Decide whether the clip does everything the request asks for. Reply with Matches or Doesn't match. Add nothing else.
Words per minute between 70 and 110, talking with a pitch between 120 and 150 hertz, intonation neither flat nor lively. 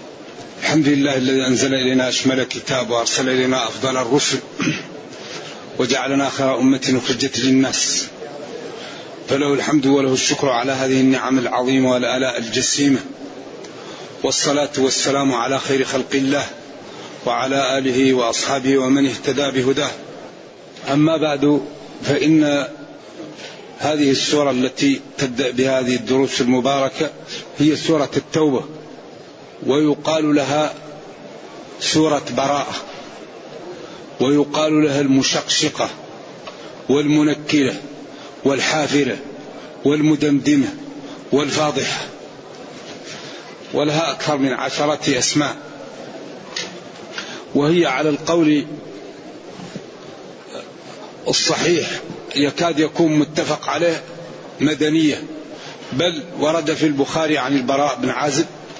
Doesn't match